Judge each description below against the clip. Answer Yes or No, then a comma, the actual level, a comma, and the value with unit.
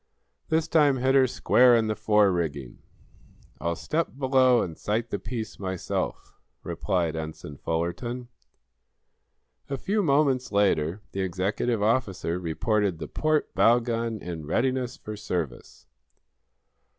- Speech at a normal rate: No, slow, 125 wpm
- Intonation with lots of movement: Yes, wide, 6.6 semitones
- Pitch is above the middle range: No, low, 110 Hz